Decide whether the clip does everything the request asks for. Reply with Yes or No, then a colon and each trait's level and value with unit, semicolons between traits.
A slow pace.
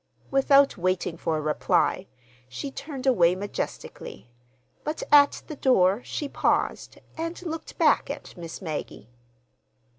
Yes: slow, 125 wpm